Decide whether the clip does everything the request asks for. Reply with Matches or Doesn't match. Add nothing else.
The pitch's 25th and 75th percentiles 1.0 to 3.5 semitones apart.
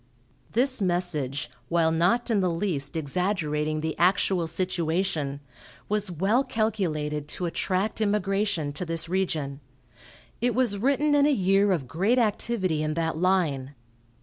Doesn't match